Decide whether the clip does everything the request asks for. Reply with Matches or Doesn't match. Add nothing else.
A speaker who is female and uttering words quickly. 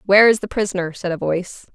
Matches